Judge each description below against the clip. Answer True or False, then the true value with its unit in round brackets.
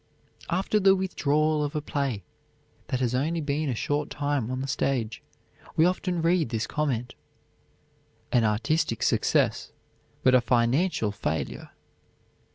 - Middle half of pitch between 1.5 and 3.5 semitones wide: False (4.5 semitones)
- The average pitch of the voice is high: False (140 Hz)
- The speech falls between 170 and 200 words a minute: False (135 wpm)